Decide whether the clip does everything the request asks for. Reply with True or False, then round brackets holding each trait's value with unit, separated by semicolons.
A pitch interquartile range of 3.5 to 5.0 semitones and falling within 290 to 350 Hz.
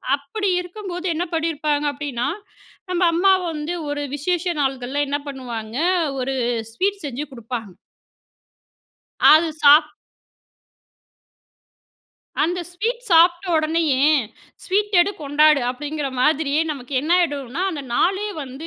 True (4.2 semitones; 300 Hz)